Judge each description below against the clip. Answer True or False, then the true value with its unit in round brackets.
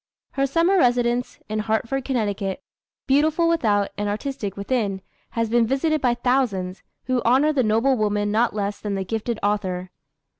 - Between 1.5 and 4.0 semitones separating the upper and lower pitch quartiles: False (4.4 semitones)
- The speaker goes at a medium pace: True (155 wpm)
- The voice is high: True (230 Hz)